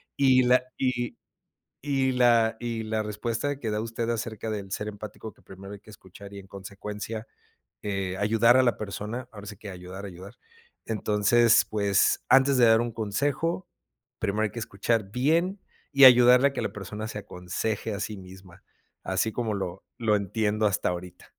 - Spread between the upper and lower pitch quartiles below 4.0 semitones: Yes, average, 3.0 semitones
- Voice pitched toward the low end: Yes, low, 110 Hz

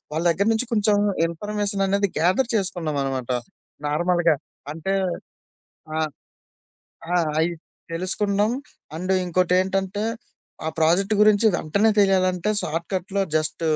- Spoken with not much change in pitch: No, average, 3.3 semitones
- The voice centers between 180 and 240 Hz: Yes, medium, 185 Hz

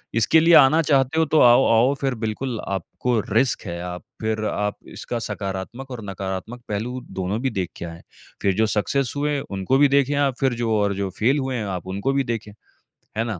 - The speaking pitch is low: Yes, low, 115 Hz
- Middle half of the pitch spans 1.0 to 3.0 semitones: No, average, 5.0 semitones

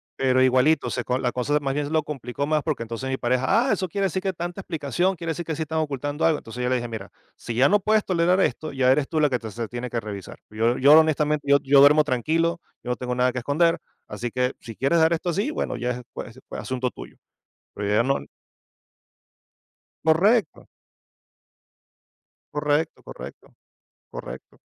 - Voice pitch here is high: No, medium, 140 Hz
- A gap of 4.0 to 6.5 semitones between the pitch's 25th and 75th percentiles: Yes, average, 4.4 semitones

